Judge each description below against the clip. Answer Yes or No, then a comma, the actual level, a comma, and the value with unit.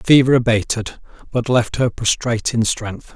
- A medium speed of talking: Yes, average, 170 wpm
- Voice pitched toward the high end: No, low, 120 Hz